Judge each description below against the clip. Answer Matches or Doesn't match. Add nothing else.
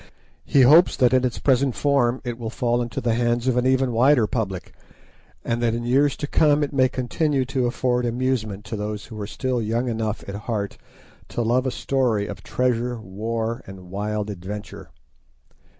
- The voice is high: Doesn't match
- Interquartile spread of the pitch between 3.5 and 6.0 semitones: Doesn't match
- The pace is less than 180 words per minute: Doesn't match